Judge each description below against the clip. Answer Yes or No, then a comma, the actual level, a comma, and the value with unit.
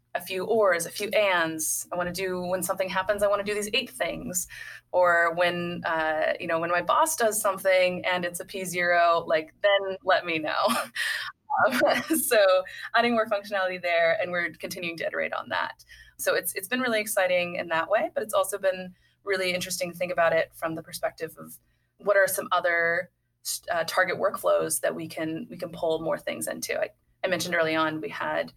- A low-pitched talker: No, medium, 180 Hz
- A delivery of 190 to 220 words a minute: Yes, fast, 205 wpm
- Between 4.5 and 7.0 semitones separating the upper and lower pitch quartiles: No, average, 2.9 semitones